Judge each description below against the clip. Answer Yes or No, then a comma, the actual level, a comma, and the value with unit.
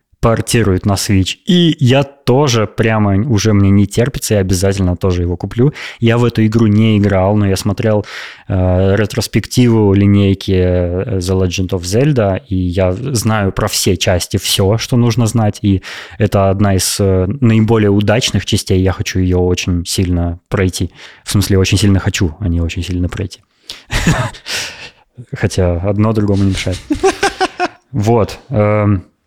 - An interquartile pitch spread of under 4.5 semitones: Yes, average, 3.2 semitones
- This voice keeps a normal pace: Yes, average, 150 wpm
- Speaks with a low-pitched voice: Yes, low, 100 Hz